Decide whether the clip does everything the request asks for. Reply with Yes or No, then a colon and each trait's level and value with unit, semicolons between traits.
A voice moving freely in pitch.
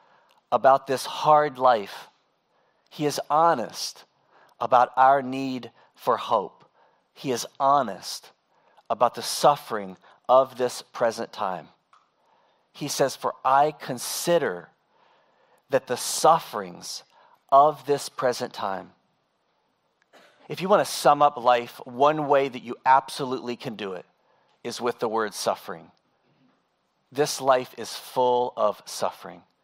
No: narrow, 2.5 semitones